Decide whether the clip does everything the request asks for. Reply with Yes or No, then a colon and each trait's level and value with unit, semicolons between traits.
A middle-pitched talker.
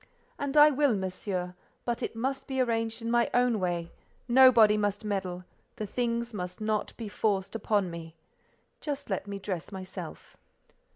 No: high, 215 Hz